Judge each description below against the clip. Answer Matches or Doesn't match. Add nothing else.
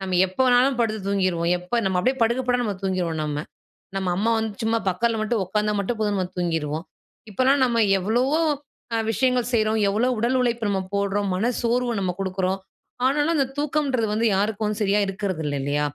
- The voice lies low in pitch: Doesn't match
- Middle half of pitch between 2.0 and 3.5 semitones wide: Doesn't match